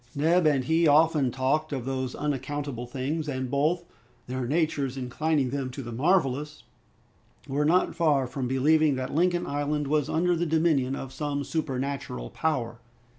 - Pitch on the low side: No, medium, 145 Hz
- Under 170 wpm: Yes, average, 155 wpm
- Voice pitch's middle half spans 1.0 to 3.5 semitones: Yes, average, 3.1 semitones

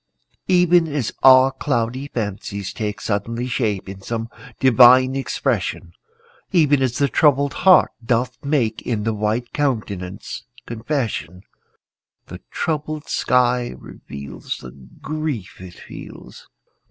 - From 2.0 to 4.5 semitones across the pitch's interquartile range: No, average, 5.0 semitones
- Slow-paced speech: Yes, slow, 115 wpm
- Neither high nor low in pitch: No, low, 120 Hz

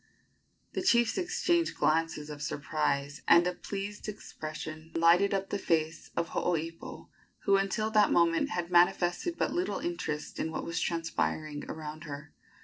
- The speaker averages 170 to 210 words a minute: No, average, 145 wpm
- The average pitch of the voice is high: No, medium, 170 Hz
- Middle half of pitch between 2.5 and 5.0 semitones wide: Yes, average, 4.3 semitones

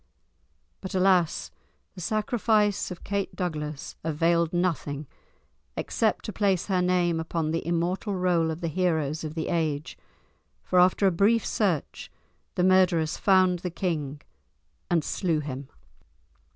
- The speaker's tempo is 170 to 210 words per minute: No, slow, 135 wpm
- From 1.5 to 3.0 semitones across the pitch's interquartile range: Yes, average, 2.7 semitones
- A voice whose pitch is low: No, medium, 175 Hz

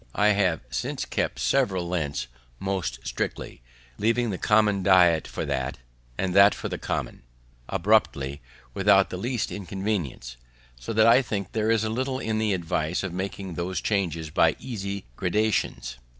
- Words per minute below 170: Yes, average, 150 wpm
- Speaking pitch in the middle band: No, very low, 95 Hz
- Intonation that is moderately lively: Yes, average, 4.0 semitones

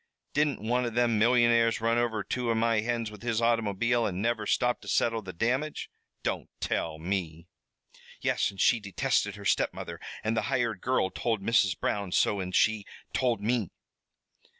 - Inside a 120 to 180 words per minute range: Yes, average, 175 wpm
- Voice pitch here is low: Yes, low, 115 Hz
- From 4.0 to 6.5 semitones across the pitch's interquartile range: No, average, 2.8 semitones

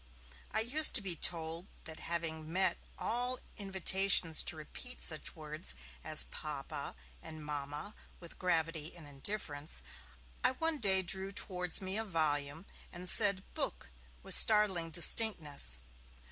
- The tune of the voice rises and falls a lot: No, average, 4.1 semitones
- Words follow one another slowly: Yes, slow, 130 wpm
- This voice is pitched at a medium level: Yes, medium, 175 Hz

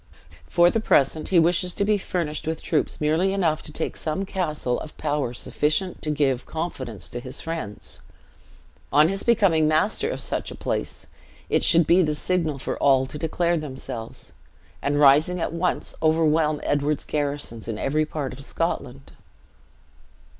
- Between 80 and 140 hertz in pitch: No, medium, 155 Hz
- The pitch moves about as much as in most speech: Yes, average, 3.3 semitones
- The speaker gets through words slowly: No, average, 160 wpm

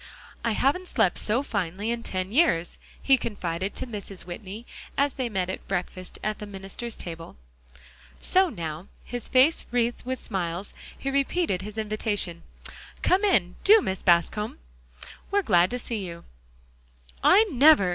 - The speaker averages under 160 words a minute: Yes, average, 150 wpm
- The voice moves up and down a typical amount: No, wide, 5.7 semitones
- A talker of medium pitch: No, high, 210 Hz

